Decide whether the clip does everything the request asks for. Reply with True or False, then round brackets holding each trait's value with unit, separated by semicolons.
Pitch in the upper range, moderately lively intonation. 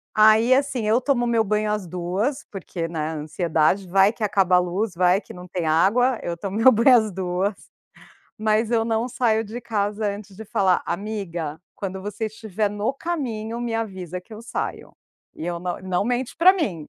True (210 Hz; 3.8 semitones)